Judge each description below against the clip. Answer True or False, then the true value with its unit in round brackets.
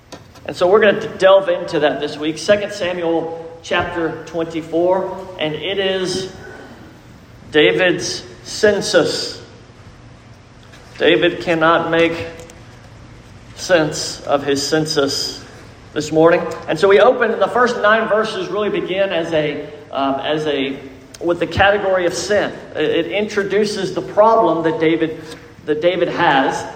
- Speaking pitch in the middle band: True (170 Hz)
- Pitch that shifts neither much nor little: True (4.0 semitones)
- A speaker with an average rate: False (130 wpm)